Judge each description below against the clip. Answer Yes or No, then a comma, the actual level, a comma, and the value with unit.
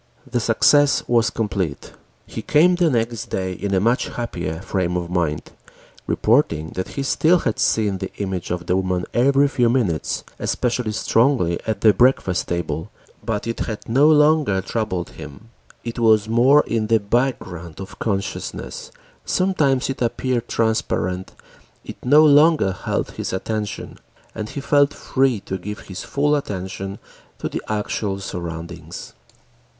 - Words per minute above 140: Yes, average, 150 wpm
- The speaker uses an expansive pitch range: Yes, wide, 5.7 semitones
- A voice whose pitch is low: Yes, low, 110 Hz